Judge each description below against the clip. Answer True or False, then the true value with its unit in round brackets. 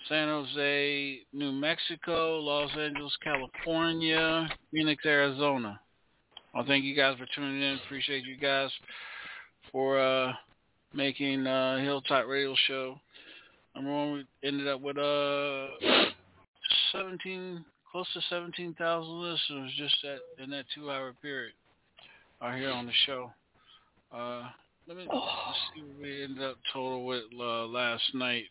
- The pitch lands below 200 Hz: True (140 Hz)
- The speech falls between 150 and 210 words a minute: False (135 wpm)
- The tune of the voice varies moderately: False (2.3 semitones)